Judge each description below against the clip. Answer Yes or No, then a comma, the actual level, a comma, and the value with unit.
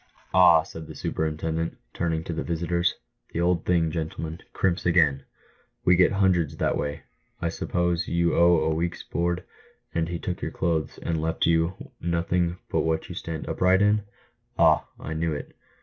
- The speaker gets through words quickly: No, average, 170 wpm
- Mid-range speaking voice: No, very low, 85 Hz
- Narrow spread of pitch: Yes, narrow, 1.4 semitones